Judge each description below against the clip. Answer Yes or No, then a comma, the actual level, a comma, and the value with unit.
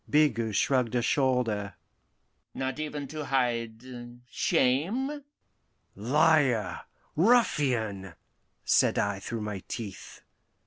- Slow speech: Yes, slow, 90 wpm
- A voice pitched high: No, low, 125 Hz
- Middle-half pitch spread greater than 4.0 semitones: Yes, average, 5.3 semitones